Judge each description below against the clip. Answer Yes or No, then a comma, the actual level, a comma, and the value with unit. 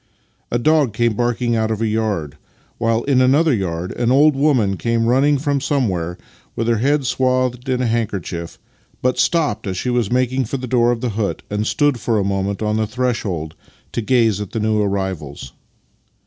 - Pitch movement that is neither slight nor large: Yes, average, 3.7 semitones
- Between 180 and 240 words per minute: Yes, average, 190 wpm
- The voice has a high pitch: No, low, 115 Hz